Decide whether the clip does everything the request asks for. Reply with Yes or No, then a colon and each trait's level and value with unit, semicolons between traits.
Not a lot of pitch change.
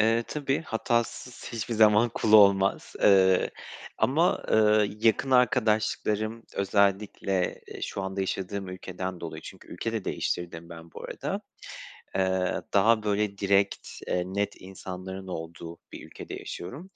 No: average, 3.0 semitones